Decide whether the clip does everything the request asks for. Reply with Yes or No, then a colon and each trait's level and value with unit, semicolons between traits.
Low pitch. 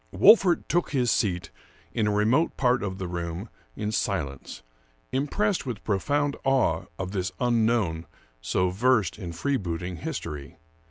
Yes: low, 105 Hz